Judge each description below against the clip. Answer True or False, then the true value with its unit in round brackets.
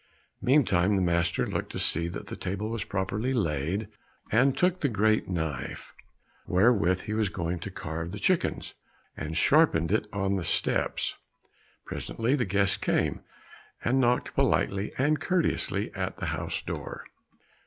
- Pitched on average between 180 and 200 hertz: False (100 Hz)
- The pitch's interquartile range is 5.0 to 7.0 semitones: True (5.6 semitones)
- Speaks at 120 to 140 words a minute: False (150 wpm)